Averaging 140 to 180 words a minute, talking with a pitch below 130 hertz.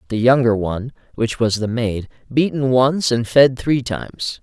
Yes: average, 175 wpm; low, 120 Hz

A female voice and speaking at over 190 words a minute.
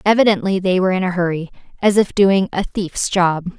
Yes: female; average, 200 wpm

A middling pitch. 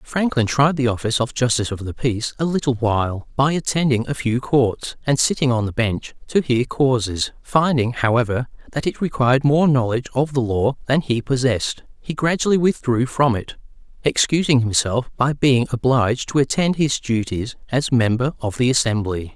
No: low, 130 Hz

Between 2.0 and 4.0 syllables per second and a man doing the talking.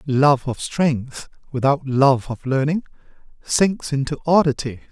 Yes: 3.9 syllables/s; male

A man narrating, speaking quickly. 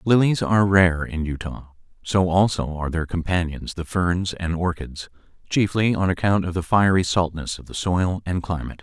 No: male; average, 175 wpm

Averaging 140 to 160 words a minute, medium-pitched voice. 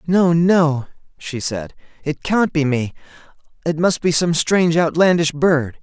Yes: average, 155 wpm; medium, 160 Hz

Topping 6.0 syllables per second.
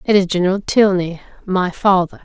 No: 5.3 syllables/s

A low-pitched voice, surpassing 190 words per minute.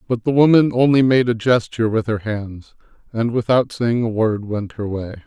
Yes: low, 115 Hz; fast, 205 wpm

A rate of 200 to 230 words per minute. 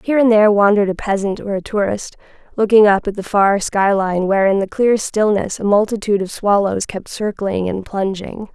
Yes: fast, 205 wpm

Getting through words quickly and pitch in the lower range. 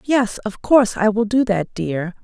No: fast, 215 wpm; high, 215 Hz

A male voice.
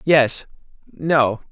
Yes: male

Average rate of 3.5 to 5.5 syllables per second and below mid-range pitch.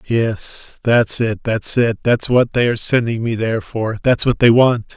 Yes: 4.4 syllables/s; low, 115 Hz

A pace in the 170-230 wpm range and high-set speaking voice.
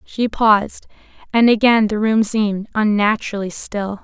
No: slow, 135 wpm; high, 215 Hz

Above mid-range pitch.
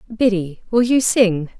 Yes: high, 210 Hz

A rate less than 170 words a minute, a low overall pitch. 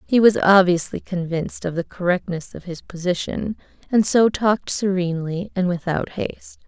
No: average, 155 wpm; medium, 185 Hz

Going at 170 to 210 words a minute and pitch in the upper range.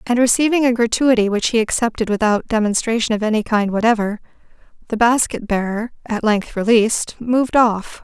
No: average, 155 wpm; high, 225 Hz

